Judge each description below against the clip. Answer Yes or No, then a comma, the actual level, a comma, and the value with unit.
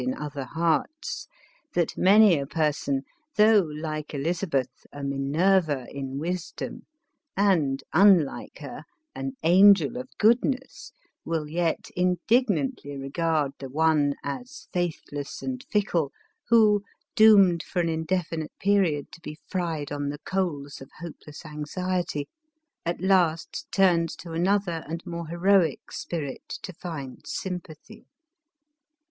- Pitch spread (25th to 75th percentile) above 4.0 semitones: Yes, average, 4.4 semitones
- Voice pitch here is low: No, medium, 165 Hz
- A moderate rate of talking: No, slow, 120 wpm